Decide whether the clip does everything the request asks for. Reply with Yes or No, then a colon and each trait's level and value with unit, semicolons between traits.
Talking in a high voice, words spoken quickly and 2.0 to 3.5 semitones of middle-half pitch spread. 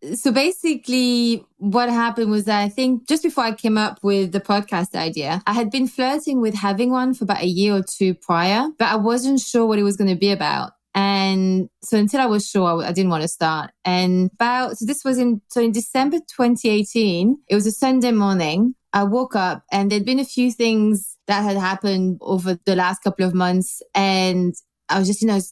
No: high, 210 Hz; fast, 215 wpm; average, 4.2 semitones